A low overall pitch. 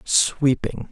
Yes: low, 110 Hz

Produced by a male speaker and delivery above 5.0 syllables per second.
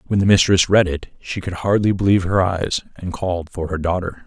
Yes: male; 5.6 syllables/s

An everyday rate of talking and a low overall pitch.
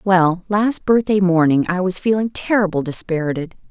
No: average, 145 wpm; medium, 185 Hz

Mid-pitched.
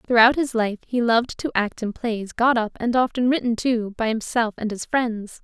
No: high, 230 Hz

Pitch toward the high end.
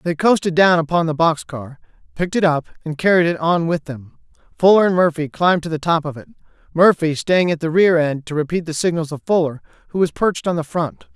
No: medium, 165 Hz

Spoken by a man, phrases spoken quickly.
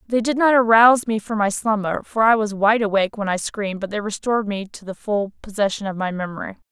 No: female; fast, 225 wpm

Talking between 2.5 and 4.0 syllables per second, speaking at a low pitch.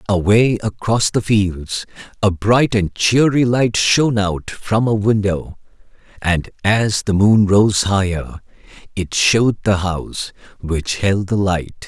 Yes: 3.7 syllables/s; low, 100 Hz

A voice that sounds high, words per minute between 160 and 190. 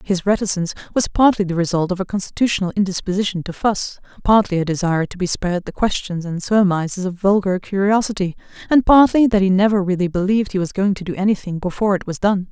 No: high, 195 Hz; average, 200 wpm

